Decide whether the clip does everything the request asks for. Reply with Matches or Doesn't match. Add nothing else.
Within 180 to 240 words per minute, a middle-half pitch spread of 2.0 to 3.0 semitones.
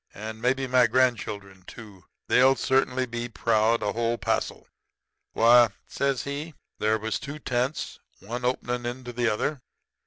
Doesn't match